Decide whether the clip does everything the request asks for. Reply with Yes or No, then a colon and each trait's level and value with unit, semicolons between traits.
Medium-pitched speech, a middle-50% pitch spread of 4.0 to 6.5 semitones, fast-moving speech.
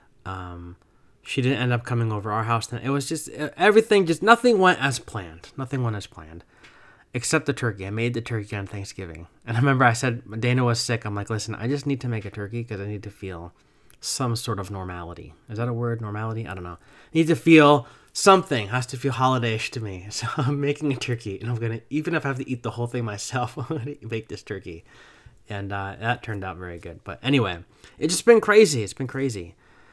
No: low, 120 Hz; average, 5.0 semitones; fast, 235 wpm